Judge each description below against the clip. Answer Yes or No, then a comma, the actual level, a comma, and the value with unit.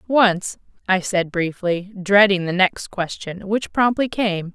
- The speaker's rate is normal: Yes, average, 145 wpm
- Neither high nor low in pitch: No, high, 195 Hz